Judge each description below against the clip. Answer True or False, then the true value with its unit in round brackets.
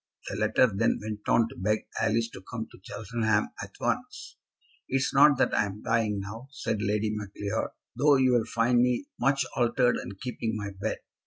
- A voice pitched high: False (110 Hz)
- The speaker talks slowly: False (190 wpm)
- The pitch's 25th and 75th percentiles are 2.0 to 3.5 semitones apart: True (3.0 semitones)